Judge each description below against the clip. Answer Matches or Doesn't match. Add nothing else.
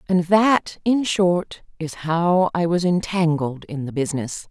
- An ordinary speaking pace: Matches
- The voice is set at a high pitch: Doesn't match